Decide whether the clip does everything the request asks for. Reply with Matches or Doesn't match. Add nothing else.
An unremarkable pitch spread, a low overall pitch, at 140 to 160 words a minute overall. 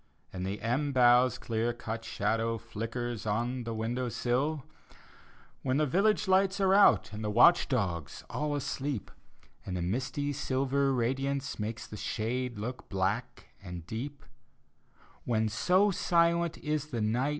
Matches